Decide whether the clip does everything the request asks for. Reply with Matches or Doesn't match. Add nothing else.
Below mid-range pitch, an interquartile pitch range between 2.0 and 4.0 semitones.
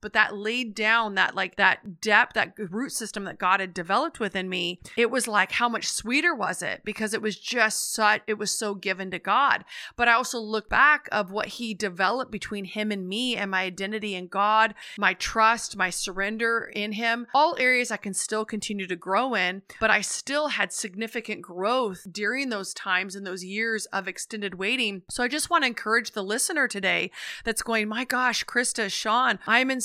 Doesn't match